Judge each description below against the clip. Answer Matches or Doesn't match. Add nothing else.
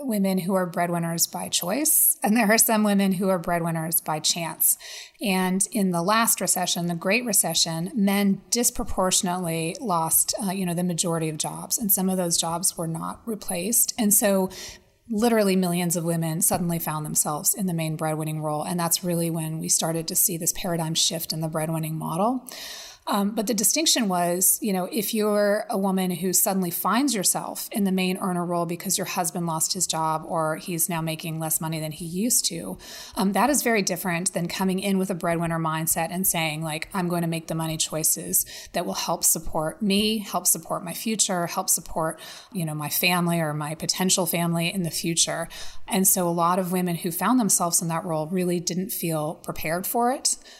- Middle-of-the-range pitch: Matches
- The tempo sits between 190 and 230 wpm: Matches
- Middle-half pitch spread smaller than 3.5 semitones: Matches